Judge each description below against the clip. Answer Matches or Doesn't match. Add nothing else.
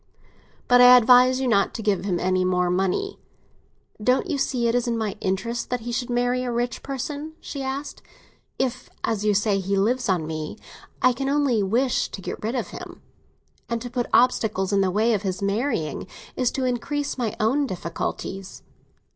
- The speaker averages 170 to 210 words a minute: Matches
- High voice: Matches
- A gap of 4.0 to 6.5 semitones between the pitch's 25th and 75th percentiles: Matches